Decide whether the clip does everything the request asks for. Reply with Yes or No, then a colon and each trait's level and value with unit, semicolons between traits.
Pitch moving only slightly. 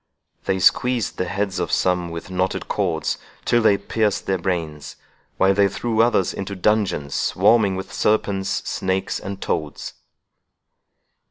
Yes: narrow, 2.3 semitones